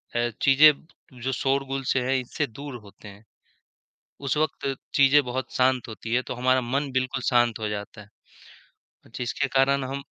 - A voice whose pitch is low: Yes, low, 130 Hz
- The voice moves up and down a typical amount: No, narrow, 2.3 semitones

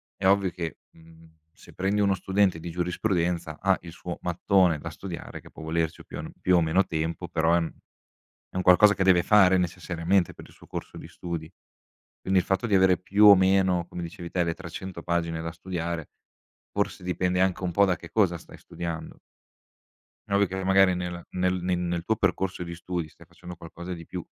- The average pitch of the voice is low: Yes, very low, 90 Hz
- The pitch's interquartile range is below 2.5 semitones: Yes, narrow, 2.1 semitones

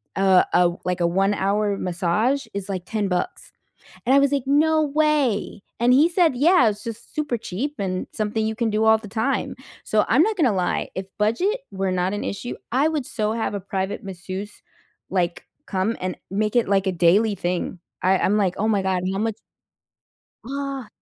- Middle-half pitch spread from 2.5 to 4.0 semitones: No, average, 5.1 semitones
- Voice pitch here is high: Yes, high, 210 Hz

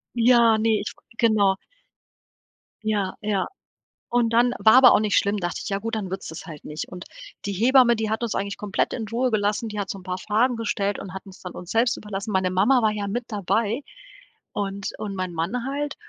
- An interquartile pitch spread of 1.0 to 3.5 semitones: Yes, average, 2.9 semitones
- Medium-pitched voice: No, high, 210 Hz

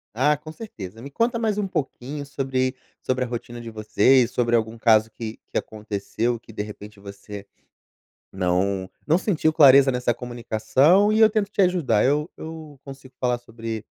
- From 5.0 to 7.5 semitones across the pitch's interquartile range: Yes, average, 5.3 semitones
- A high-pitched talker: No, low, 125 Hz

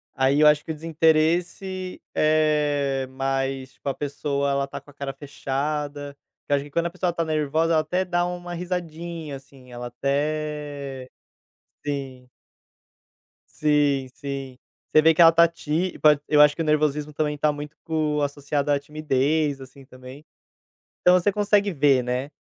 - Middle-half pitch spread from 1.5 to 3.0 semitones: Yes, narrow, 2.5 semitones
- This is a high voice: No, medium, 150 Hz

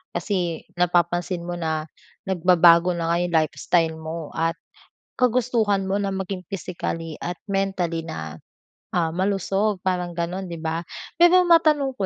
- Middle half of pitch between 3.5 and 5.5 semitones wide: No, average, 2.8 semitones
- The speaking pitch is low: No, medium, 175 Hz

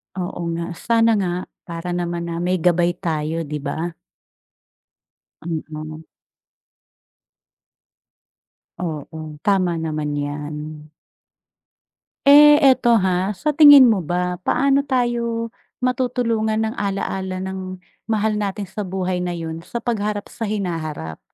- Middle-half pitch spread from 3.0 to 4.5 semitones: No, average, 5.1 semitones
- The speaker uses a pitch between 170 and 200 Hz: Yes, medium, 185 Hz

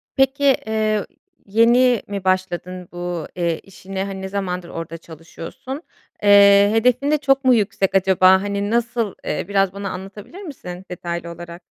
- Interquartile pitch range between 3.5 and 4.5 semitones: Yes, average, 3.8 semitones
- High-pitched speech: Yes, high, 195 Hz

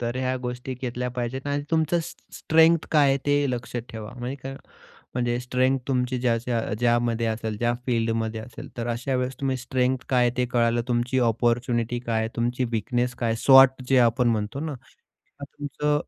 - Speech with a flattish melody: Yes, narrow, 2.0 semitones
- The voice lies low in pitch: Yes, low, 125 Hz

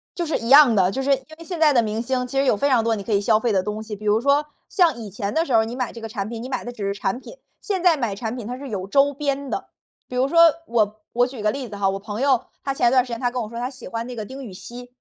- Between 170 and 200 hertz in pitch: No, high, 240 Hz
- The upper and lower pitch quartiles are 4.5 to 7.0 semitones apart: No, average, 4.1 semitones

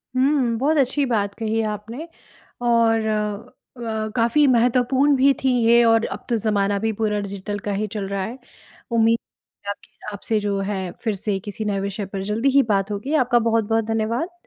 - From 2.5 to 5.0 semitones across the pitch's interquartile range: Yes, average, 2.9 semitones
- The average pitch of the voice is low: No, high, 225 Hz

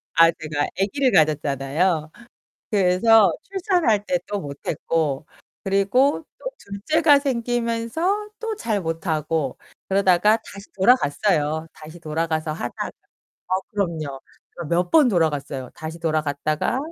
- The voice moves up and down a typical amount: No, wide, 6.8 semitones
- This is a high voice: No, medium, 180 Hz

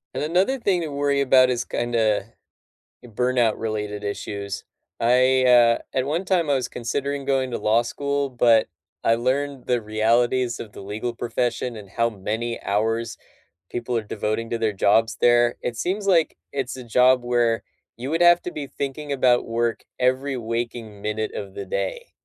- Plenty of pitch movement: No, average, 3.1 semitones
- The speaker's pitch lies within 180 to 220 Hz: No, low, 120 Hz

